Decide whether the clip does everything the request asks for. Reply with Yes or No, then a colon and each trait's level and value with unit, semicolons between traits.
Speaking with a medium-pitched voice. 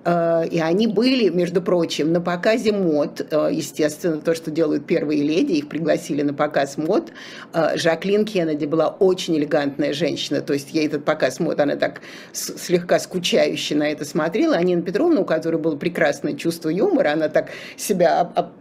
Yes: medium, 165 Hz